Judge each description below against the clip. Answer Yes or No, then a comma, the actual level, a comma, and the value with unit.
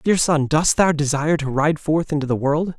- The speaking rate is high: Yes, fast, 235 wpm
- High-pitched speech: No, medium, 150 Hz